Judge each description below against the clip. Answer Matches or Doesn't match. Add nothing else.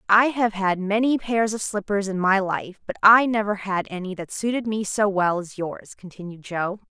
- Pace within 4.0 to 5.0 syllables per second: Matches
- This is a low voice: Doesn't match